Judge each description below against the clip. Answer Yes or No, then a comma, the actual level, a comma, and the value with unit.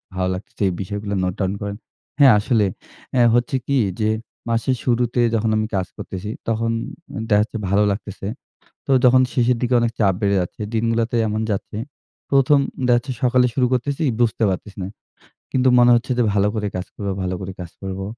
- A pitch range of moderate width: Yes, average, 3.5 semitones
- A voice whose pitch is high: No, low, 110 Hz